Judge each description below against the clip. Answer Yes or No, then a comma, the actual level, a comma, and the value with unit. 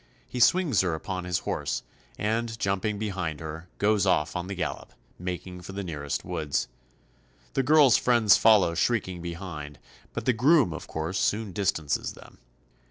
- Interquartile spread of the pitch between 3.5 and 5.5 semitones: Yes, average, 4.5 semitones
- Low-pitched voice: Yes, very low, 95 Hz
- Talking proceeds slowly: No, average, 160 wpm